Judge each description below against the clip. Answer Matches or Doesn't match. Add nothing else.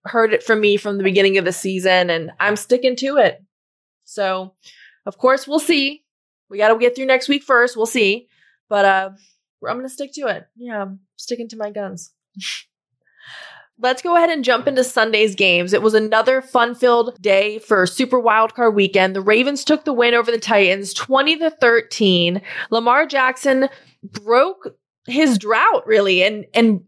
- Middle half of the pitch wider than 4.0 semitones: Matches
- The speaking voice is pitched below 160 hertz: Doesn't match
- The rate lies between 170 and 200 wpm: Matches